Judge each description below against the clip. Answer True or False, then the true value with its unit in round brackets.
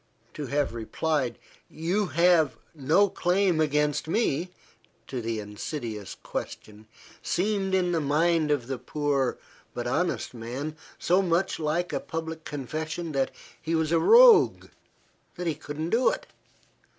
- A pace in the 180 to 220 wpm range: False (140 wpm)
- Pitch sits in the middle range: True (155 Hz)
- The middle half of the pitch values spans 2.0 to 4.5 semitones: True (4.0 semitones)